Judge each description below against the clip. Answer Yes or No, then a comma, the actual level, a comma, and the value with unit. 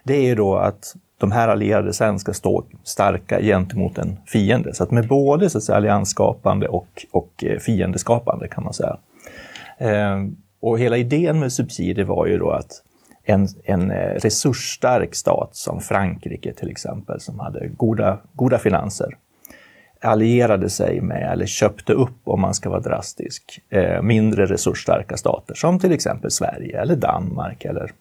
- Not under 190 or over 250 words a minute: No, average, 150 wpm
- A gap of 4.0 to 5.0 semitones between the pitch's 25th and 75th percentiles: Yes, average, 4.5 semitones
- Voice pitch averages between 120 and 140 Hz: No, low, 110 Hz